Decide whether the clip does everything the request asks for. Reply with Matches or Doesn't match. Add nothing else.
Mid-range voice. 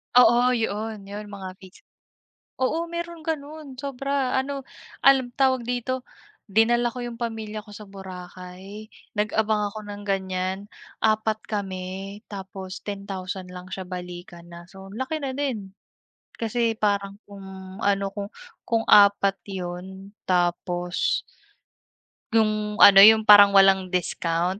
Doesn't match